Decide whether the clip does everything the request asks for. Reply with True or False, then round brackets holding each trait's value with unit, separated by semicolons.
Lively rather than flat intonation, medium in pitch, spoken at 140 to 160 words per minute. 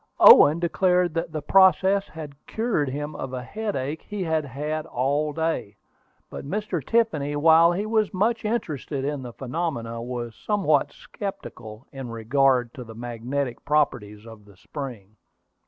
True (6.0 semitones; 145 Hz; 150 wpm)